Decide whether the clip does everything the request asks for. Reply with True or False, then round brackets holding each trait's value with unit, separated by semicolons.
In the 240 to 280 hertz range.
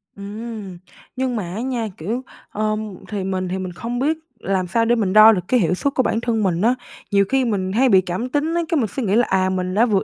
False (215 Hz)